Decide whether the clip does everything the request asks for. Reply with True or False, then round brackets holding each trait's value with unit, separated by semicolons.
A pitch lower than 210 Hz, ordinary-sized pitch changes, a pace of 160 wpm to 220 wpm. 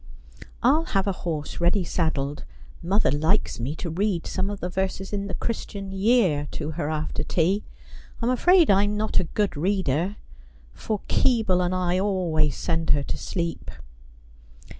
True (185 Hz; 4.2 semitones; 170 wpm)